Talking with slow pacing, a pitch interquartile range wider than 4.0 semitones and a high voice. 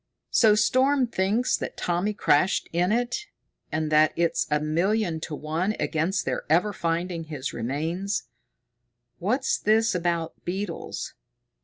No: slow, 130 wpm; average, 4.9 semitones; medium, 180 Hz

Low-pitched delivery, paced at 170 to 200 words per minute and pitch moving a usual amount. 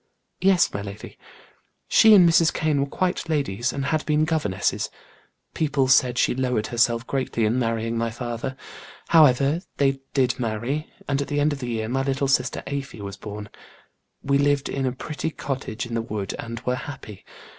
Yes: low, 130 Hz; average, 175 wpm; average, 3.7 semitones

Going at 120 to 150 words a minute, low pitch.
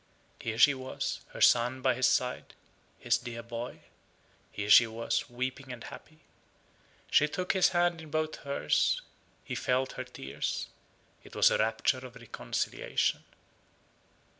Yes: average, 140 wpm; low, 130 Hz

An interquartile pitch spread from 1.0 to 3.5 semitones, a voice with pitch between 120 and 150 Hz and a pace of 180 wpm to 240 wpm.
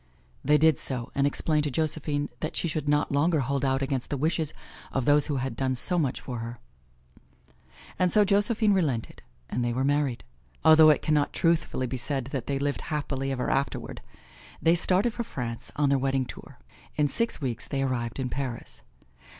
Yes: average, 3.1 semitones; medium, 140 Hz; average, 190 wpm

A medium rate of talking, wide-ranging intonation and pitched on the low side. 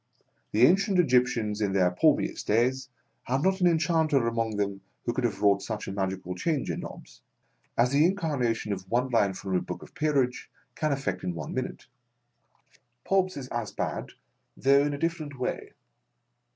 Yes: average, 180 wpm; wide, 6.4 semitones; low, 125 Hz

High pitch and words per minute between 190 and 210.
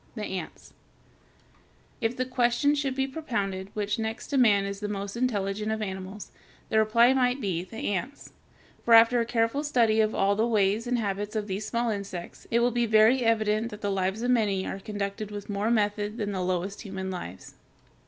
Yes: high, 215 Hz; average, 195 wpm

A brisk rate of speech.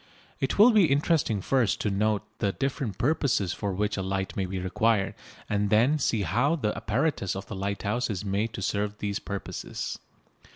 No: average, 180 wpm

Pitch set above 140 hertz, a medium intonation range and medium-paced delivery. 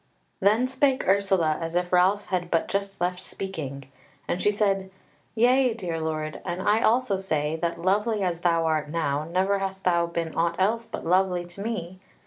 Yes: medium, 185 Hz; average, 3.1 semitones; average, 180 wpm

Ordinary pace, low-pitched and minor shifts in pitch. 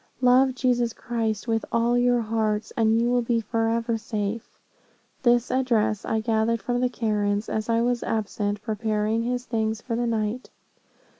No: average, 160 wpm; high, 230 Hz; narrow, 1.8 semitones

